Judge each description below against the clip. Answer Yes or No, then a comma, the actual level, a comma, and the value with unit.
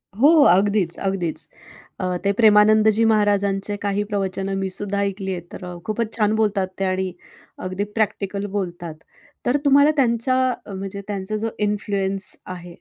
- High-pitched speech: Yes, high, 200 Hz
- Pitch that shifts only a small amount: Yes, narrow, 2.1 semitones